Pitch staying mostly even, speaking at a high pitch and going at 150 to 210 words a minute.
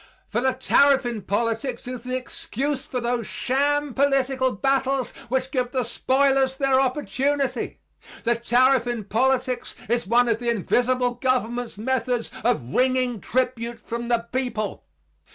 No: narrow, 1.9 semitones; very high, 250 Hz; average, 140 wpm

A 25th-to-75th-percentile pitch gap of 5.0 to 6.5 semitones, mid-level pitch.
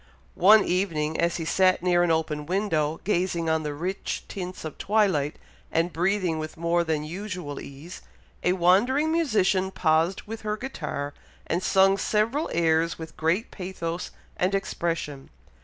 No: average, 3.4 semitones; medium, 175 Hz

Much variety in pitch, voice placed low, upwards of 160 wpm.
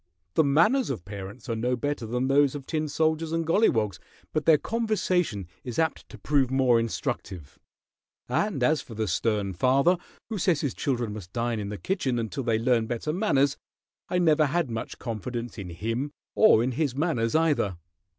Yes: wide, 5.7 semitones; low, 130 Hz; average, 180 wpm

